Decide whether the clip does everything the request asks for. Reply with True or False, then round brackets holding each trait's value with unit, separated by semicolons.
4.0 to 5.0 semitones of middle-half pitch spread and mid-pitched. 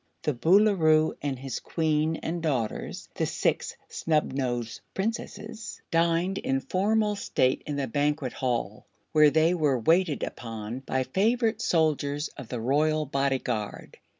True (4.4 semitones; 150 Hz)